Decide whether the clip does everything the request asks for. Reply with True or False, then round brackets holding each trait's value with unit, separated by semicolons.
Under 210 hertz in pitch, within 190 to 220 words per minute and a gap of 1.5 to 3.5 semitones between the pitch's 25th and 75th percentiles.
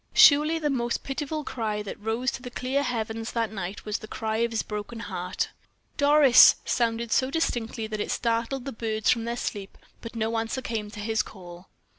False (230 Hz; 195 wpm; 2.8 semitones)